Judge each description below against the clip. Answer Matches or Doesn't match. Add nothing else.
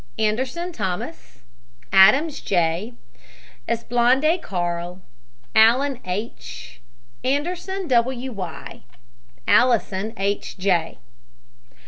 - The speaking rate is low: Matches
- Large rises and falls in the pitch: Matches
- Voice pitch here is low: Doesn't match